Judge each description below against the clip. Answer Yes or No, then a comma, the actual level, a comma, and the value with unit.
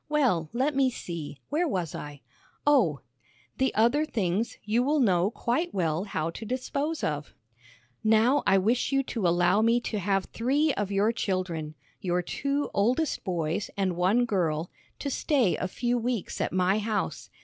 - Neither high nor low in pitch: No, high, 210 Hz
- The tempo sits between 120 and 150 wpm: No, average, 165 wpm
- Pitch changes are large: Yes, wide, 6.2 semitones